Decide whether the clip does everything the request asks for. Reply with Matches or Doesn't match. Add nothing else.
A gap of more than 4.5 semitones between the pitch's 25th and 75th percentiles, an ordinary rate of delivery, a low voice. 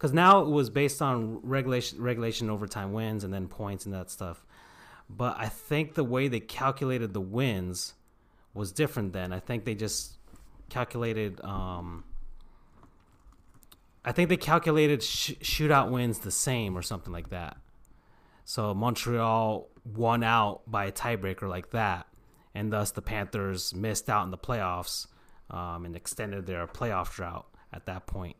Matches